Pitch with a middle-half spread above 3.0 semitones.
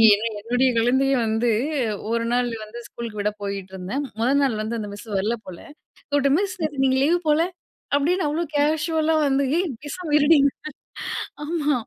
Yes: average, 4.6 semitones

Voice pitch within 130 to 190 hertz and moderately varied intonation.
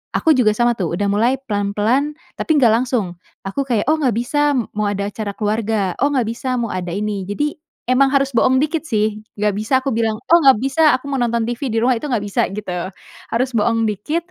No: high, 230 Hz; average, 4.3 semitones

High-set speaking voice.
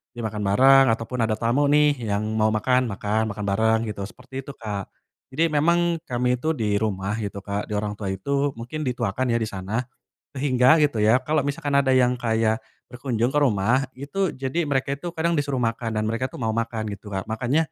No: low, 120 Hz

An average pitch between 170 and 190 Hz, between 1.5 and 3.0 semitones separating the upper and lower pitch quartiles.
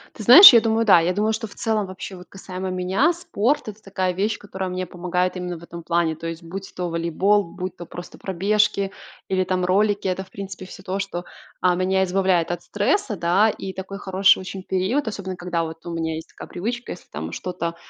Yes: medium, 185 Hz; narrow, 2.4 semitones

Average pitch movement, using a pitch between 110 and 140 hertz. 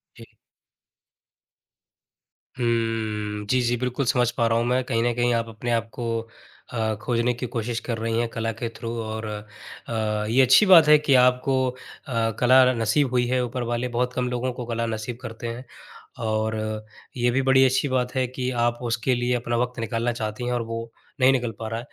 No: narrow, 1.8 semitones; low, 120 Hz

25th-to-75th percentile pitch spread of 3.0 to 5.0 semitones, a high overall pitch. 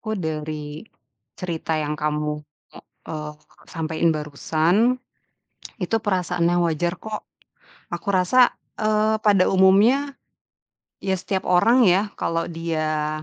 No: average, 4.6 semitones; medium, 175 Hz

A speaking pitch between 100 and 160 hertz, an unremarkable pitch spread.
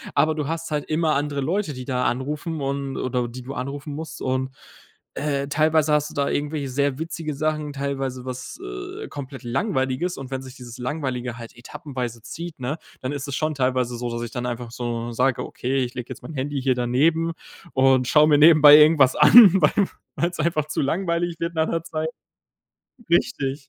Yes: medium, 140 Hz; average, 3.4 semitones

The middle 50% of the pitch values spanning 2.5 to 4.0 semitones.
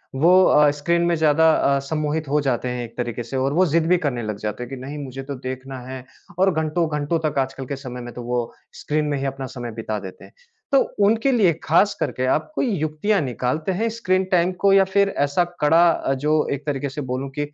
No: average, 4.5 semitones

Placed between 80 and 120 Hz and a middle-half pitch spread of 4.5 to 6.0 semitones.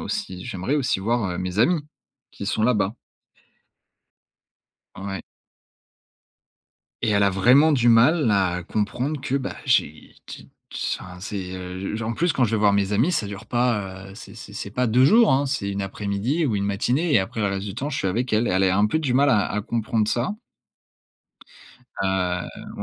Yes: low, 105 Hz; average, 4.8 semitones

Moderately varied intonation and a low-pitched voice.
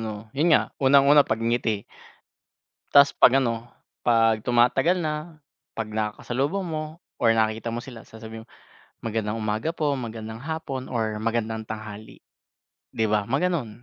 Yes: average, 4.2 semitones; low, 115 Hz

